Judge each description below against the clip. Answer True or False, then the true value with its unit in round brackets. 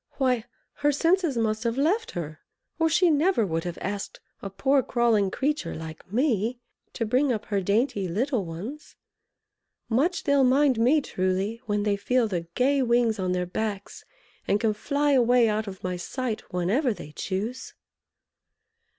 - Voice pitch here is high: True (230 Hz)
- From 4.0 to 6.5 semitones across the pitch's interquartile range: True (5.5 semitones)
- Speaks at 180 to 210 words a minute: False (160 wpm)